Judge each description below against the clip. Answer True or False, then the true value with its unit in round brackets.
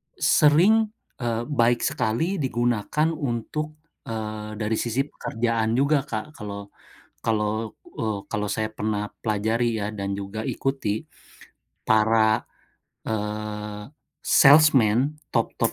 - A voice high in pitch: False (110 Hz)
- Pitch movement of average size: True (4.2 semitones)